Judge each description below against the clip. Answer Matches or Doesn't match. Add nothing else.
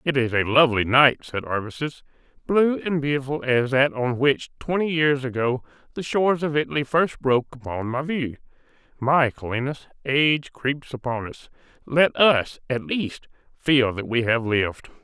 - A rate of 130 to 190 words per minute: Matches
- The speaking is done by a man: Matches